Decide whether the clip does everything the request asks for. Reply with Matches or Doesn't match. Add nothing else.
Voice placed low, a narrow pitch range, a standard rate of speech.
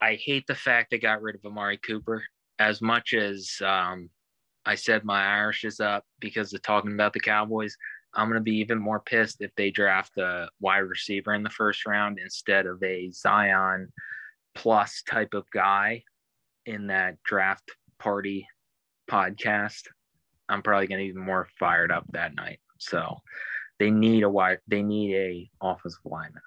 Matches